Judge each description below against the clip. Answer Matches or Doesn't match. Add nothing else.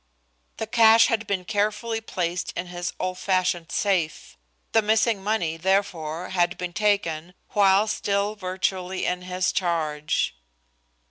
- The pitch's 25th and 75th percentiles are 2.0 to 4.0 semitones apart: Matches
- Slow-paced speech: Matches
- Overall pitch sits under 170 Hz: Doesn't match